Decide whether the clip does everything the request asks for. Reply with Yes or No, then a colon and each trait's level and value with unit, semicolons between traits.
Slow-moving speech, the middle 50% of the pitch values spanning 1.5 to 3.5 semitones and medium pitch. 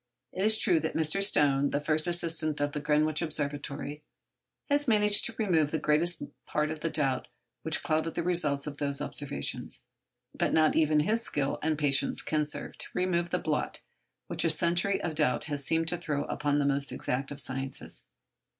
No: average, 190 wpm; average, 2.8 semitones; medium, 155 Hz